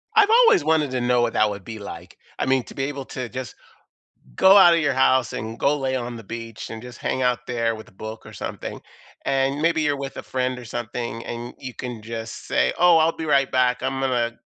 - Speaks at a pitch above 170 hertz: No, low, 125 Hz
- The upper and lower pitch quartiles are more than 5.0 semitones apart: No, average, 3.0 semitones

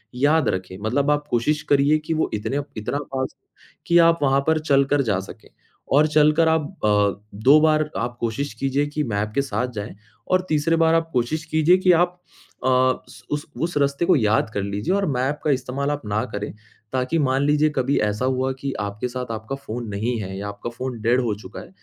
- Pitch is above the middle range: No, low, 135 Hz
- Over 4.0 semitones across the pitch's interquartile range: Yes, average, 4.7 semitones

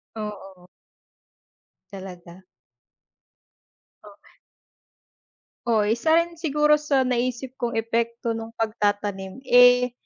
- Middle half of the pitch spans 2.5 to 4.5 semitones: Yes, average, 3.7 semitones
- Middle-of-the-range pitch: No, high, 230 Hz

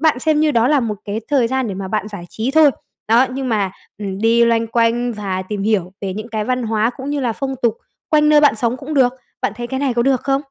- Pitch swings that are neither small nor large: Yes, average, 3.9 semitones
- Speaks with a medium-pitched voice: No, high, 235 Hz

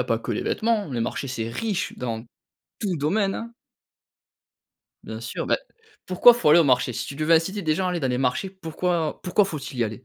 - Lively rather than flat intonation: Yes, wide, 6.8 semitones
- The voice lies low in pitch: No, medium, 165 Hz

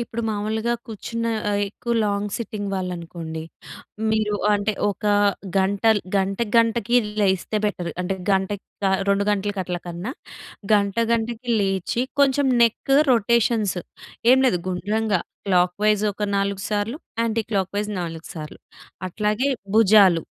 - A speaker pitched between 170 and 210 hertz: Yes, high, 205 Hz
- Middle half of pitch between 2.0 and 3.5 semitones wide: Yes, average, 2.7 semitones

